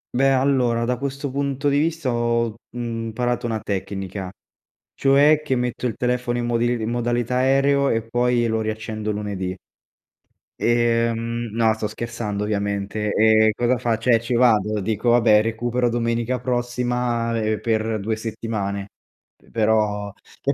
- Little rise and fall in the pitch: Yes, narrow, 2.1 semitones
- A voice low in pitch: Yes, low, 115 Hz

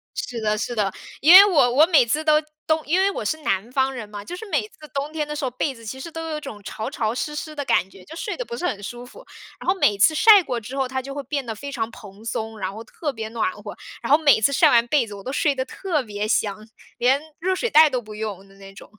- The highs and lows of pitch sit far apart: Yes, wide, 6.0 semitones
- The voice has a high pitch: Yes, very high, 260 Hz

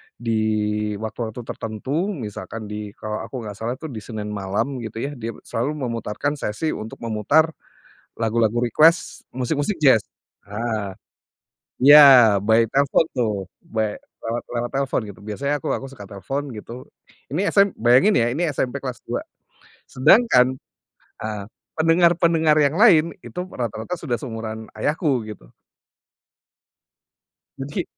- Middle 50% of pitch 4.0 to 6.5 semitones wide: Yes, average, 4.9 semitones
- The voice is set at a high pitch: No, low, 120 Hz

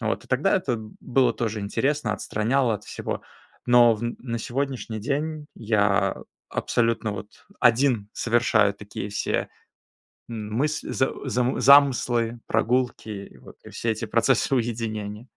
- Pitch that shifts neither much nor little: Yes, average, 3.2 semitones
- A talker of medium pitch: No, low, 115 Hz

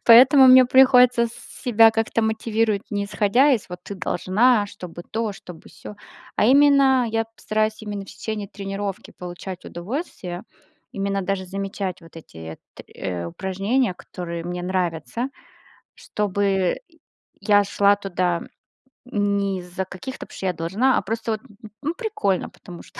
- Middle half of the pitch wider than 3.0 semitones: Yes, average, 3.9 semitones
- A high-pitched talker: Yes, high, 200 Hz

